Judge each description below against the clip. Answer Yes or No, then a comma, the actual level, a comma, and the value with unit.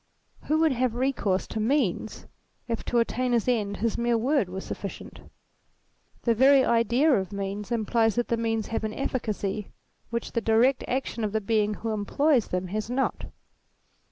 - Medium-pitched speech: No, high, 230 Hz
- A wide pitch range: No, average, 3.0 semitones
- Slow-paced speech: No, average, 175 wpm